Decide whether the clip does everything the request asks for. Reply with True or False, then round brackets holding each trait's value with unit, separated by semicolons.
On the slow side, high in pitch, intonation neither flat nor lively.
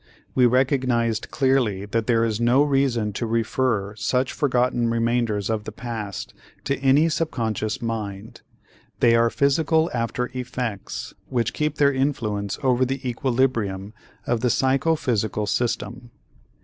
False (130 wpm; 120 Hz; 3.1 semitones)